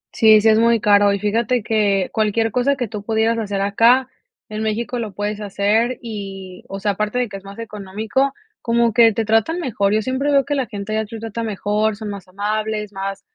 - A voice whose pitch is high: Yes, high, 215 Hz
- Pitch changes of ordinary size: No, narrow, 2.2 semitones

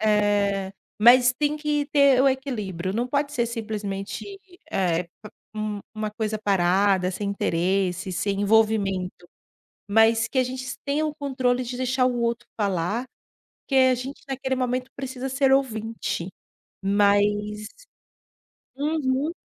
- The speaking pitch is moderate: No, high, 225 Hz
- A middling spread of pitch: Yes, average, 4.5 semitones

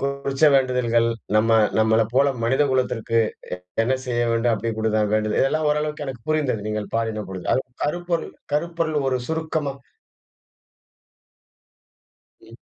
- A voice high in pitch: No, low, 130 Hz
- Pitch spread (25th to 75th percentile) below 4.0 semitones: No, average, 4.7 semitones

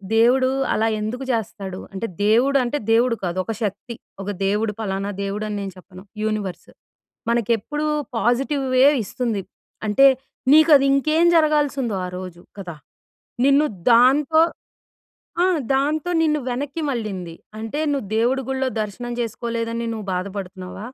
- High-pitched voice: Yes, high, 230 Hz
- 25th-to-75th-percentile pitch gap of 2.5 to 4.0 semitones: No, average, 5.1 semitones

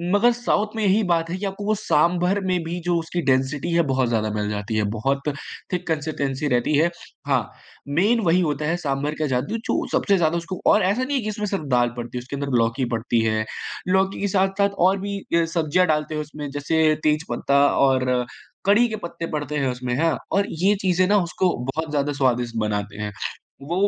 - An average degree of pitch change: No, wide, 6.0 semitones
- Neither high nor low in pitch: Yes, medium, 160 Hz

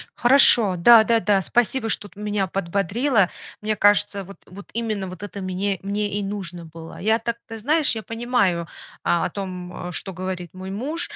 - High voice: Yes, high, 200 Hz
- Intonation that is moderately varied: Yes, average, 3.4 semitones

